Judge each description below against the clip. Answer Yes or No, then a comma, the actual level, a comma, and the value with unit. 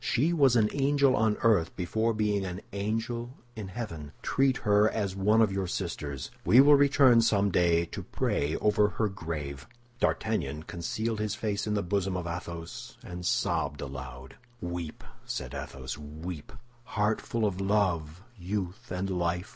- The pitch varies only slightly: No, average, 4.7 semitones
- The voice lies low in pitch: Yes, low, 100 Hz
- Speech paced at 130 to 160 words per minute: Yes, average, 155 wpm